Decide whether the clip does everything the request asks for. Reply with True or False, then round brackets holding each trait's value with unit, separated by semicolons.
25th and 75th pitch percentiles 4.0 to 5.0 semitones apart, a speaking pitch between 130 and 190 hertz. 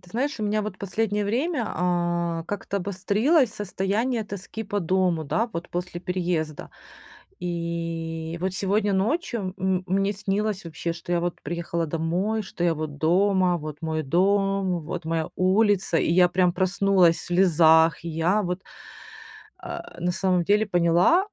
False (3.1 semitones; 185 Hz)